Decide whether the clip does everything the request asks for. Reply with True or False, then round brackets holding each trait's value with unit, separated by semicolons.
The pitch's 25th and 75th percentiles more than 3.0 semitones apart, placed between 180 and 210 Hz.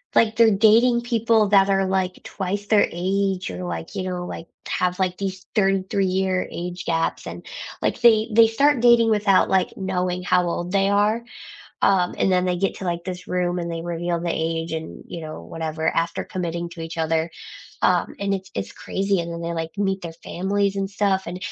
False (2.7 semitones; 185 Hz)